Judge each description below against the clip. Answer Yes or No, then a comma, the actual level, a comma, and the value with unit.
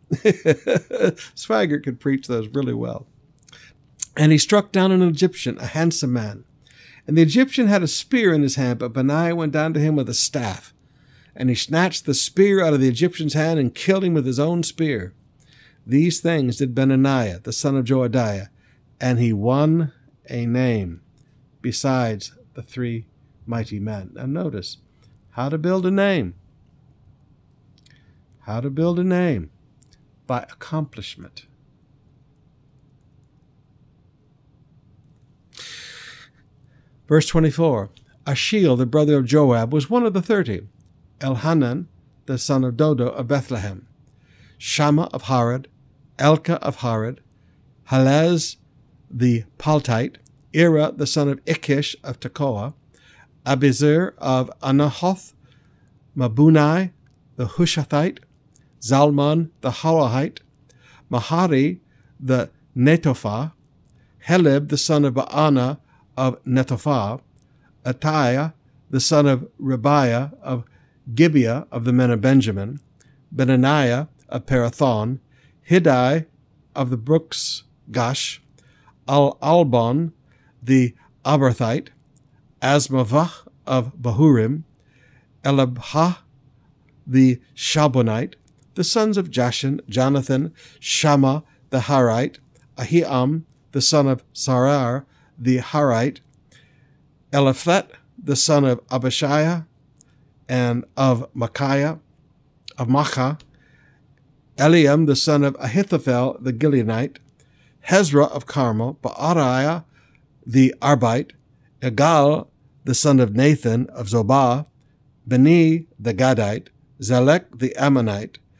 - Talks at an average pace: No, slow, 110 wpm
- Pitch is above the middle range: No, low, 135 Hz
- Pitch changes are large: No, average, 2.9 semitones